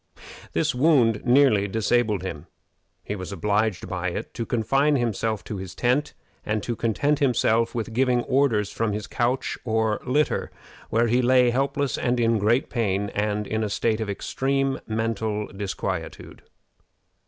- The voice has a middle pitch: No, low, 115 Hz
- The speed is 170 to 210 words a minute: No, average, 155 wpm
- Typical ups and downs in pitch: Yes, average, 3.1 semitones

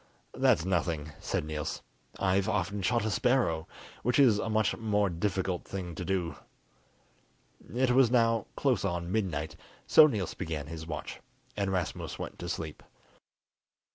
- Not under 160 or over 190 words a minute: No, average, 145 wpm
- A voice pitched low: Yes, very low, 95 Hz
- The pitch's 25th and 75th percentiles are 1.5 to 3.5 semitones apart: No, average, 4.7 semitones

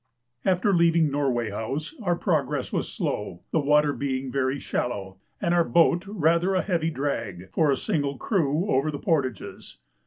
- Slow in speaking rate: No, average, 160 wpm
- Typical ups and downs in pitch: Yes, average, 4.4 semitones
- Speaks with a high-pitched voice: No, medium, 145 Hz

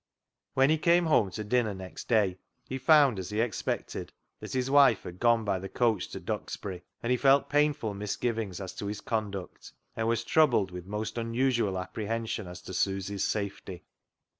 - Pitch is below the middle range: Yes, low, 110 Hz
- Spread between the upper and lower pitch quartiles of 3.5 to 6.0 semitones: Yes, average, 4.3 semitones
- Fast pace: No, average, 180 wpm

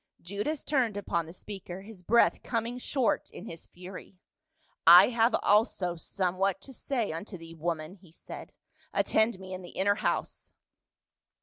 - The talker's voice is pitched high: Yes, high, 195 Hz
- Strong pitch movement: No, average, 4.4 semitones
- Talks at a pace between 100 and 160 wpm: Yes, average, 155 wpm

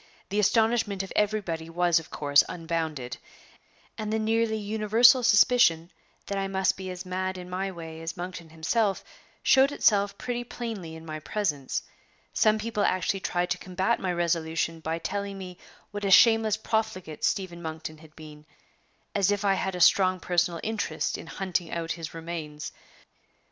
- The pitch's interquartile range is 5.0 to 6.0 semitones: No, average, 4.2 semitones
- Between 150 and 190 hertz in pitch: Yes, medium, 185 Hz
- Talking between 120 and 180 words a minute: Yes, average, 165 wpm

